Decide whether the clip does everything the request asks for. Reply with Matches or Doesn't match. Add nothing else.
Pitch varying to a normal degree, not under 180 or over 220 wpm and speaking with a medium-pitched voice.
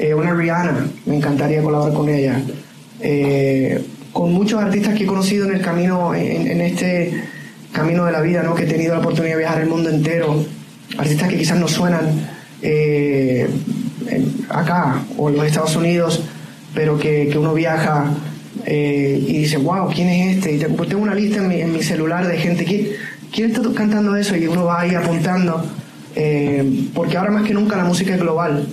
Matches